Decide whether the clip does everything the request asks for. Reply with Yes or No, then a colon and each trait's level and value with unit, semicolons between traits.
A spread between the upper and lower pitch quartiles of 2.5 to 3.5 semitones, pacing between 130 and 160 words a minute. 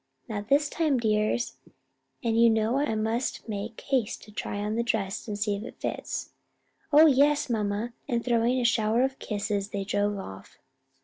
No: average, 3.0 semitones; average, 180 wpm